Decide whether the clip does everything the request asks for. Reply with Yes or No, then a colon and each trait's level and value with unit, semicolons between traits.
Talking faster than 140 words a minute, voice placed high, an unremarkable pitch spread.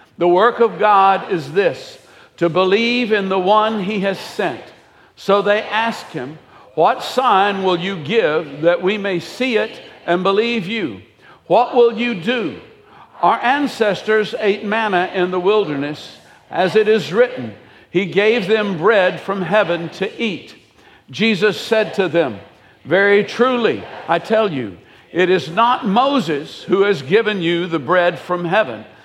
Yes: average, 155 wpm; high, 200 Hz; average, 3.5 semitones